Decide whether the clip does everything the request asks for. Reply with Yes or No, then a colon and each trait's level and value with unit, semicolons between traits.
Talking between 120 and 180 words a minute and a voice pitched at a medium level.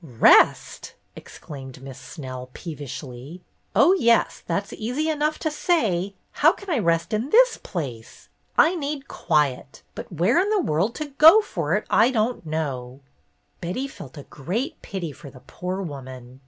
Yes: average, 155 wpm; medium, 175 Hz